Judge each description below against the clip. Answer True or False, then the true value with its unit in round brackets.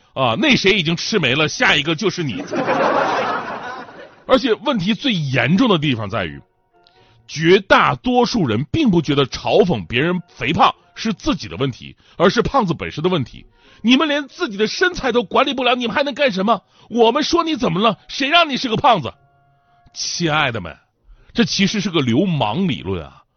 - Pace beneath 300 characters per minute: True (265 characters per minute)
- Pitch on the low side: False (190 Hz)